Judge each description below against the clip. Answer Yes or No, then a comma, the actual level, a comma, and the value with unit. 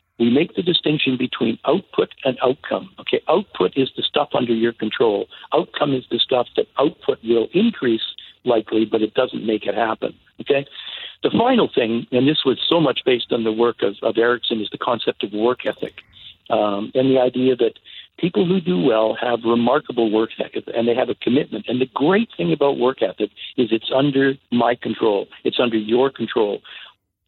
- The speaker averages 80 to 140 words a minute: No, average, 190 wpm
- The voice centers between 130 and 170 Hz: No, low, 120 Hz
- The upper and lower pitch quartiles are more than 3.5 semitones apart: No, average, 2.8 semitones